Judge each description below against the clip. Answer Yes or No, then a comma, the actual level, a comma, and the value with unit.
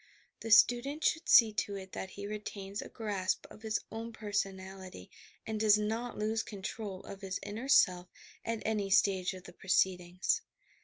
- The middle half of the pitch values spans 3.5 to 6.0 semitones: No, narrow, 2.6 semitones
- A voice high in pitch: Yes, high, 205 Hz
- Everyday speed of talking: Yes, average, 165 wpm